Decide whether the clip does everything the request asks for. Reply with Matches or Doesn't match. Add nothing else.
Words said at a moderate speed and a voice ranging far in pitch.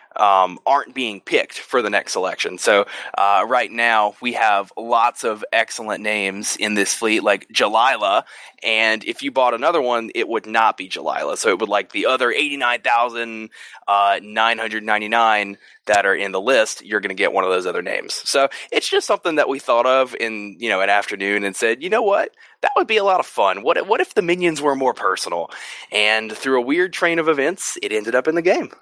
Doesn't match